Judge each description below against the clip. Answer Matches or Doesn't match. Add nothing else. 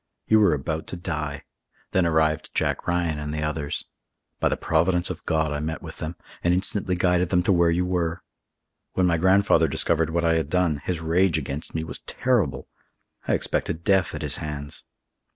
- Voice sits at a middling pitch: Doesn't match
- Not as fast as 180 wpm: Doesn't match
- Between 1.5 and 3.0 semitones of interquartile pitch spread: Matches